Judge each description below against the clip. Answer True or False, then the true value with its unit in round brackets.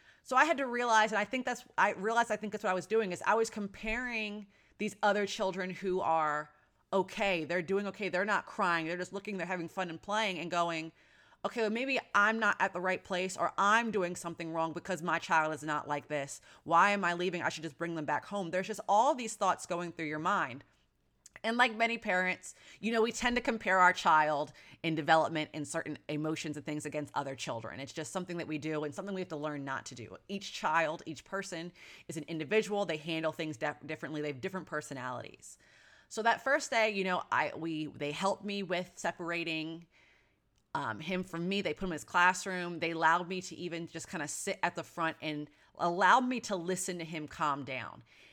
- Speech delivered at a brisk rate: True (225 wpm)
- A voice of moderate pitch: True (175 Hz)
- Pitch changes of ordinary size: True (4.2 semitones)